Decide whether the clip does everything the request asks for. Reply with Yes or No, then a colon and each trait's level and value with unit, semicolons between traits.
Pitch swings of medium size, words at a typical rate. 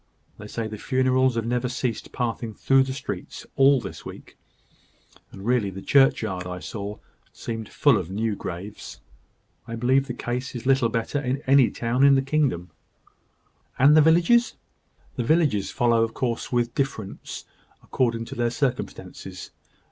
Yes: average, 3.2 semitones; average, 160 wpm